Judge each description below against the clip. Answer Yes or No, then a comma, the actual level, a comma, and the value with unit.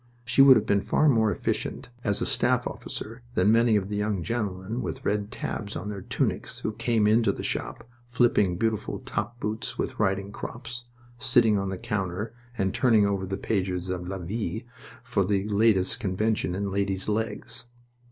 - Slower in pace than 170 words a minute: No, average, 180 wpm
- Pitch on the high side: No, low, 105 Hz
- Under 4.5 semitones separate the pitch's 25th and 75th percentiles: Yes, average, 2.9 semitones